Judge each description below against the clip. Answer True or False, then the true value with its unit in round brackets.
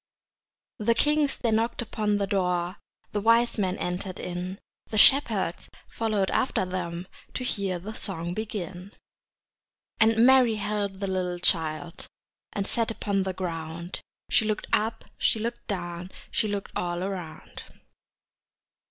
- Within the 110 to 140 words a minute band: True (135 wpm)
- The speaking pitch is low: False (195 Hz)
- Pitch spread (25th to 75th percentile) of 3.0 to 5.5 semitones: True (3.6 semitones)